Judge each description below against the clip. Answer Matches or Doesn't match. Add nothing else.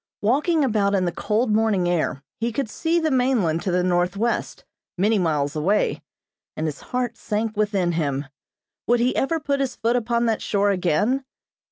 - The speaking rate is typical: Matches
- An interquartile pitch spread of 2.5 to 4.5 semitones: Doesn't match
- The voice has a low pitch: Doesn't match